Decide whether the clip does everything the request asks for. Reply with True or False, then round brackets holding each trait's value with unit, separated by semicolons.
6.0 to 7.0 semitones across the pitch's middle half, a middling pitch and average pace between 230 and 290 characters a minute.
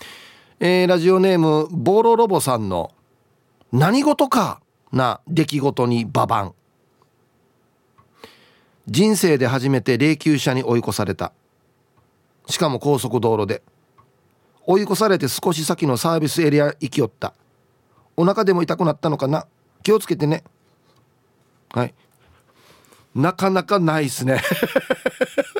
True (6.3 semitones; 150 Hz; 235 characters per minute)